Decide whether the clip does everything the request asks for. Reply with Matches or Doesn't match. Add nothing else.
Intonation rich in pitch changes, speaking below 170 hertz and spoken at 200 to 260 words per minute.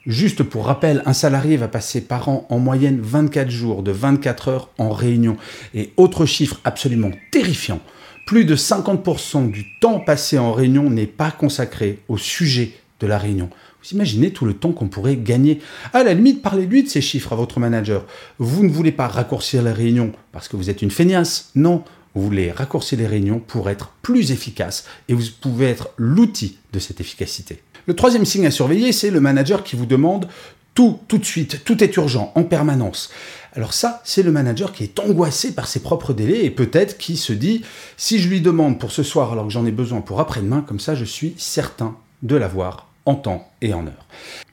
Matches